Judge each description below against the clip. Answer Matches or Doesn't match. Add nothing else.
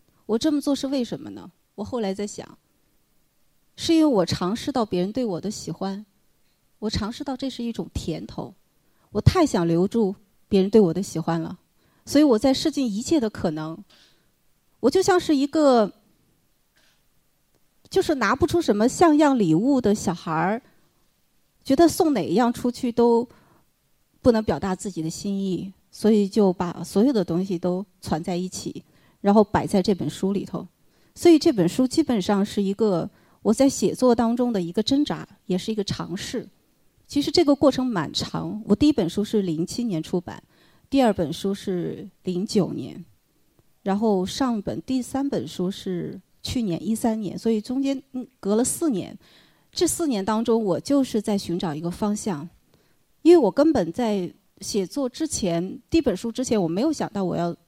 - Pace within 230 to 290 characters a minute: Matches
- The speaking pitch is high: Matches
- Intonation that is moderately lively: Doesn't match